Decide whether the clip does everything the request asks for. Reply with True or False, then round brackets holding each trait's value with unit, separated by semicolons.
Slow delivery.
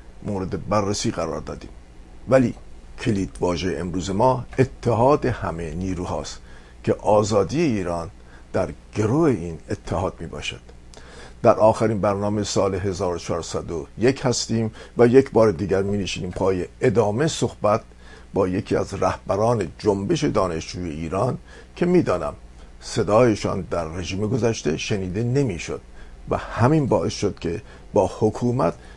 False (120 wpm)